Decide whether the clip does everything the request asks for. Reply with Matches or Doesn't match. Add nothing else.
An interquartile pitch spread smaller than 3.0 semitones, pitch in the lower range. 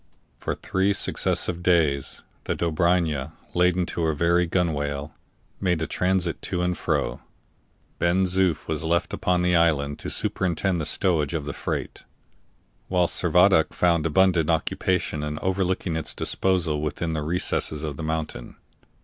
Matches